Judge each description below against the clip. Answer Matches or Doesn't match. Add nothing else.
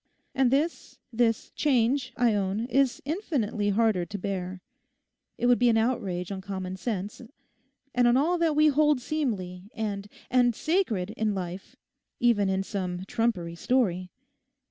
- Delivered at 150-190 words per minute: Doesn't match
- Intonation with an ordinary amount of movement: Matches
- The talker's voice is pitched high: Matches